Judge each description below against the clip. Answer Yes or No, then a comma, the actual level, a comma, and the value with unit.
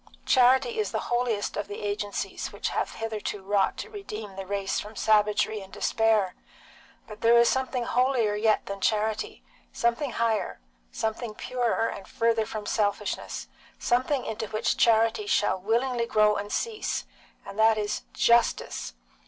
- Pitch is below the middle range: No, high, 220 Hz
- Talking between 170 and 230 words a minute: No, average, 150 wpm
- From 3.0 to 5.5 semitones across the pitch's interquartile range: No, narrow, 2.4 semitones